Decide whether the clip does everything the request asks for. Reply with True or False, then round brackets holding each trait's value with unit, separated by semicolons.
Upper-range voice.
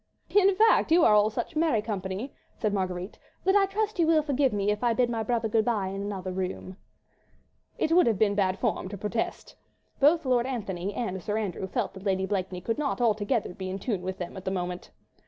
True (210 Hz)